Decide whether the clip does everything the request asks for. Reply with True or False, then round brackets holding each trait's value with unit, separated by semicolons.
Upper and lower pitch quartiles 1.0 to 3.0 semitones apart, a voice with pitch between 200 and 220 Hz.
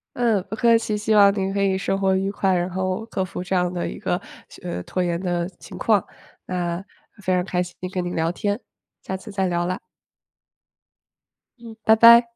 False (2.7 semitones; 190 Hz)